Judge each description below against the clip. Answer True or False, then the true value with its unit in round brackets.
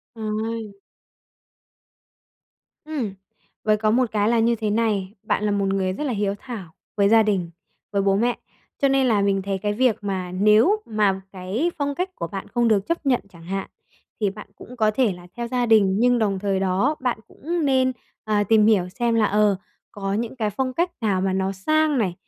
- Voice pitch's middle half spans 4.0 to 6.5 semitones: False (3.6 semitones)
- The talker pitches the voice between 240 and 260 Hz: False (215 Hz)